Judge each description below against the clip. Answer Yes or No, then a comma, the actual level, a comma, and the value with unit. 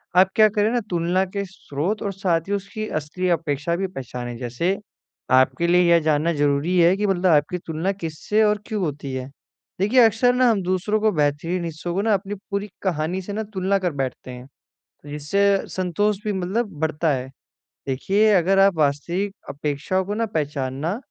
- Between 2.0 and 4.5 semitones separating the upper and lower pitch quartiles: No, average, 5.0 semitones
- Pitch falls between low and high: Yes, medium, 180 Hz